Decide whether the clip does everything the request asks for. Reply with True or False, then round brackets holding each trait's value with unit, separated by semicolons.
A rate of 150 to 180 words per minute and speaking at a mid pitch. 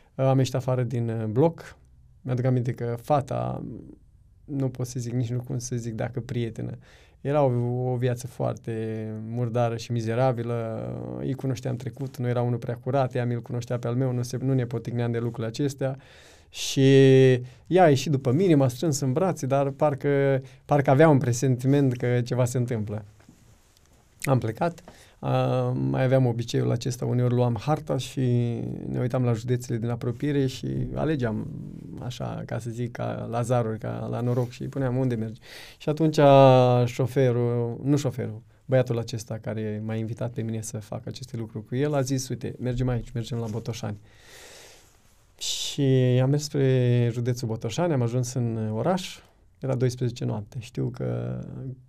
False (170 wpm; 125 Hz)